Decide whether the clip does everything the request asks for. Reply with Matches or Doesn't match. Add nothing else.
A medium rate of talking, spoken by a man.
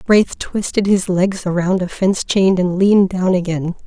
Doesn't match